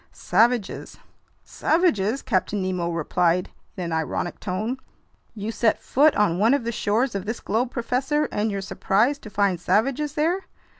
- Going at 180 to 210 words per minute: No, average, 155 wpm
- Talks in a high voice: Yes, high, 215 Hz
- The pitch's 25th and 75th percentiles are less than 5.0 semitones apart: No, wide, 5.4 semitones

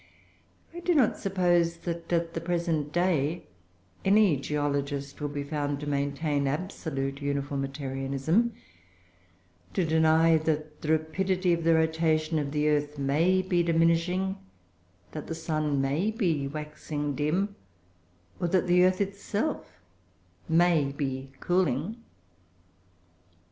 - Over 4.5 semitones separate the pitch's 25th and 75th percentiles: No, average, 3.6 semitones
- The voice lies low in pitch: No, medium, 160 Hz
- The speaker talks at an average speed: No, slow, 120 wpm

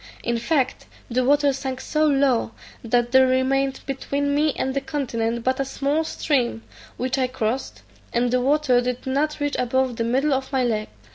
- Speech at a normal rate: Yes, average, 185 wpm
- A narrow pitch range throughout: Yes, narrow, 2.3 semitones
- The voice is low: No, very high, 260 Hz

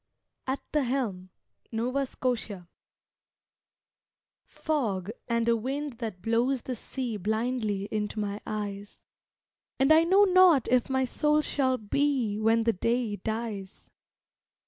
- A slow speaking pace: Yes, slow, 125 wpm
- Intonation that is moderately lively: Yes, average, 4.1 semitones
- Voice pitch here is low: No, high, 235 Hz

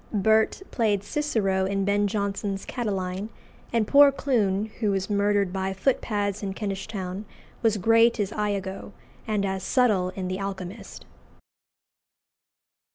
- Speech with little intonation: Yes, narrow, 2.3 semitones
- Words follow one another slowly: Yes, slow, 130 wpm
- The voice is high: Yes, high, 200 Hz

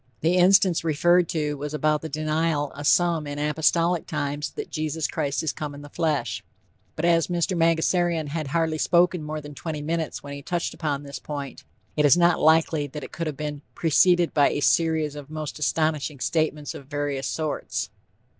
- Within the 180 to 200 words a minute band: Yes, average, 190 wpm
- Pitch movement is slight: Yes, narrow, 2.3 semitones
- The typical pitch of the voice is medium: Yes, medium, 155 Hz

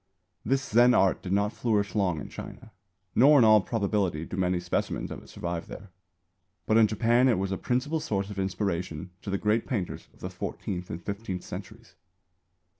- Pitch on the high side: No, low, 100 Hz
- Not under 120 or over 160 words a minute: No, average, 190 wpm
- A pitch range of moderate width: Yes, average, 3.8 semitones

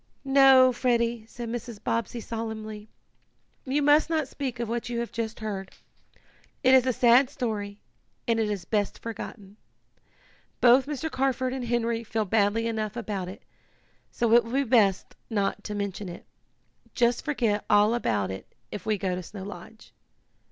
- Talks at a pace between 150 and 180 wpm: Yes, average, 160 wpm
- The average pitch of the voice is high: Yes, high, 230 Hz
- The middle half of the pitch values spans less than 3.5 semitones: Yes, average, 3.1 semitones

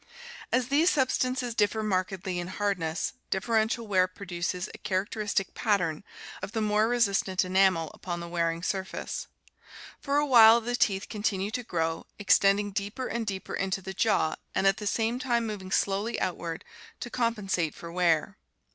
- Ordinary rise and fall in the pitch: Yes, average, 3.5 semitones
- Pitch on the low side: No, high, 200 Hz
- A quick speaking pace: No, average, 165 wpm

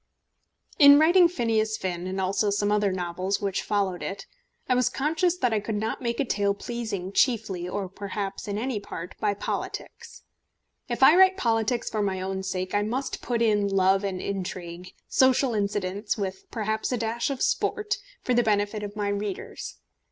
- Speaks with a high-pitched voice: Yes, high, 205 Hz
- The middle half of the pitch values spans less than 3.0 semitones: No, average, 3.6 semitones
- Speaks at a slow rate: No, average, 180 wpm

